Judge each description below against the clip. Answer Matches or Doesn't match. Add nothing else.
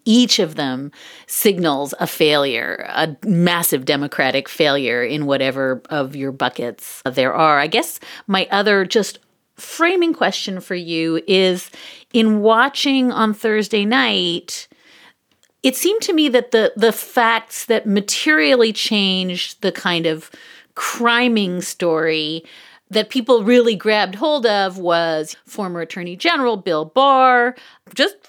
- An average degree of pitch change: Doesn't match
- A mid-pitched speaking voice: Doesn't match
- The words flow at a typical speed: Doesn't match